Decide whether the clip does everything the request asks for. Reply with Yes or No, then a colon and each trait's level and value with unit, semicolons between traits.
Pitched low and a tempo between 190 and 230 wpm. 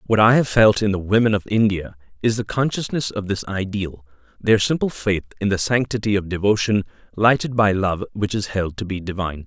Yes: low, 100 Hz; average, 195 wpm